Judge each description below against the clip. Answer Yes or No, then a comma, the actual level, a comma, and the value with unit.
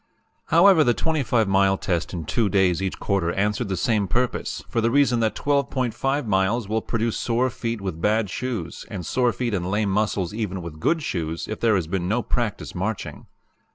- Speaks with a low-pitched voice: Yes, low, 110 Hz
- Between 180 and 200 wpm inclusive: Yes, average, 190 wpm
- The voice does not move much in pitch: No, average, 4.0 semitones